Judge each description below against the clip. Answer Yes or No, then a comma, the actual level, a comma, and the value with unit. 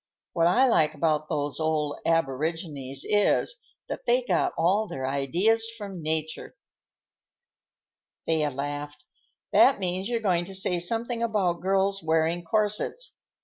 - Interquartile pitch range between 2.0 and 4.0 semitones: No, average, 5.2 semitones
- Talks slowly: Yes, slow, 130 wpm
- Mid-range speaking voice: Yes, medium, 170 Hz